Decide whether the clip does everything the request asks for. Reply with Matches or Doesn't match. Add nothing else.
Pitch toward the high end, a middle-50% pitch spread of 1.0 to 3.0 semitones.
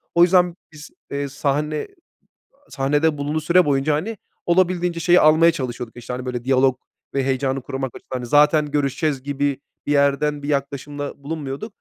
Doesn't match